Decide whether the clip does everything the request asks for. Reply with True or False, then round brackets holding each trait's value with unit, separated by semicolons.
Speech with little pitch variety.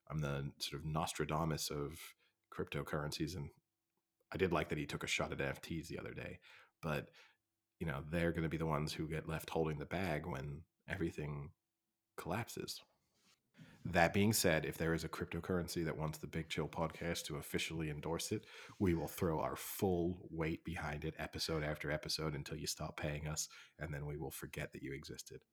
True (1.9 semitones)